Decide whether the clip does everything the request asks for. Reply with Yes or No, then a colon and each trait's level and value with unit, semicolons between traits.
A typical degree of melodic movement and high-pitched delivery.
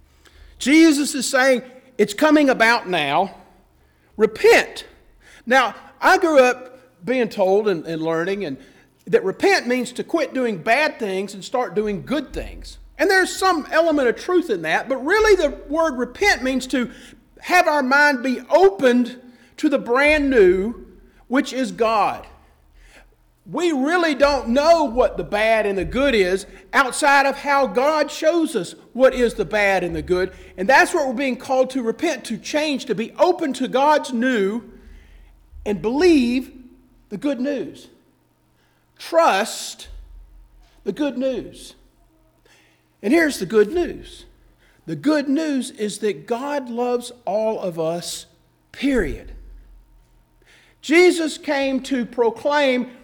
No: wide, 6.2 semitones; very high, 255 Hz